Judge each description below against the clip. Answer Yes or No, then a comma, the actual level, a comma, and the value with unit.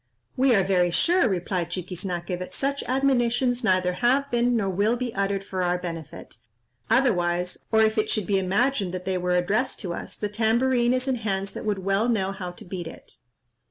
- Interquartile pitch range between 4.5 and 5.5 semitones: Yes, average, 4.9 semitones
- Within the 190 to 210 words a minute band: Yes, average, 195 wpm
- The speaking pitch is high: Yes, high, 200 Hz